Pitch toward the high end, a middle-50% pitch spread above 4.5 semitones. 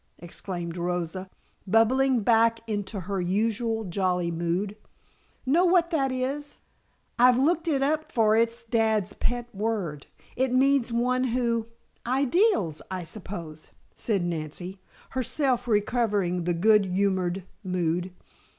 Yes: high, 220 Hz; wide, 5.6 semitones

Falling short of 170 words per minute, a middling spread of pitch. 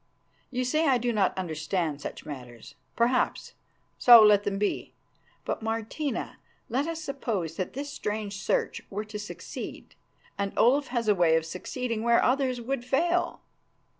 Yes: average, 155 wpm; average, 4.7 semitones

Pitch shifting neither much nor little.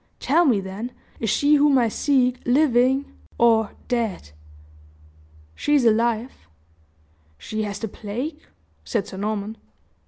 Yes: average, 3.9 semitones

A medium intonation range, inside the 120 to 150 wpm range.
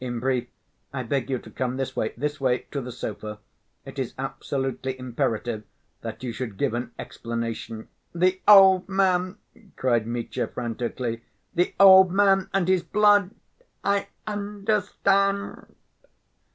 No: wide, 8.2 semitones; average, 140 wpm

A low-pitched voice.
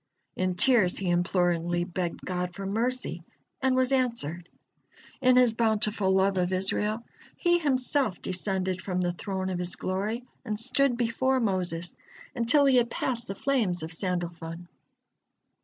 No: high, 195 Hz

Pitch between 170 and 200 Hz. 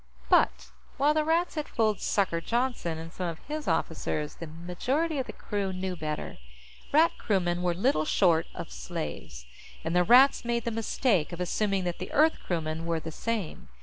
Yes: medium, 185 Hz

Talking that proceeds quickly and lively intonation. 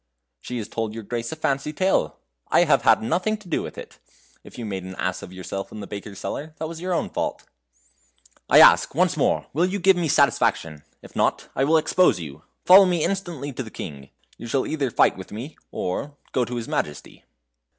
Yes: fast, 215 wpm; wide, 8.5 semitones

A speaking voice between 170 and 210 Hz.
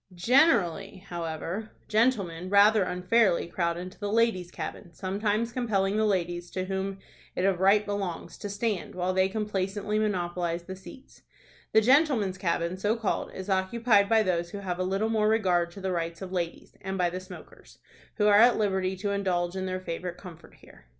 Yes: high, 190 Hz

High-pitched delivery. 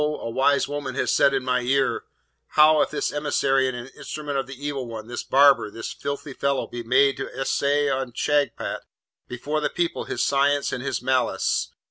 No: low, 135 Hz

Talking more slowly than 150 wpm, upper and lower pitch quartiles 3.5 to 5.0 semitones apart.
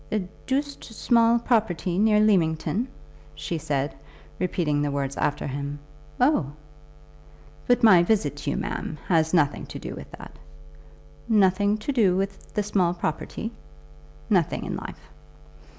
No: slow, 135 wpm; wide, 5.6 semitones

